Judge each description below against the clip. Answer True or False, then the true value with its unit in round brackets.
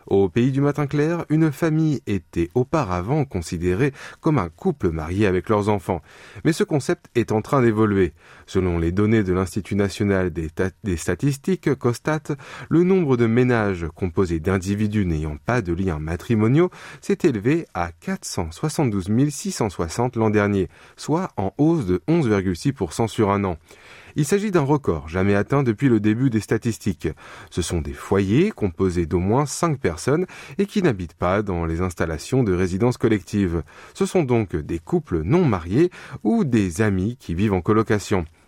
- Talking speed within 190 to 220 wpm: False (165 wpm)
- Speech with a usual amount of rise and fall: False (7.8 semitones)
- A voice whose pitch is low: True (110 Hz)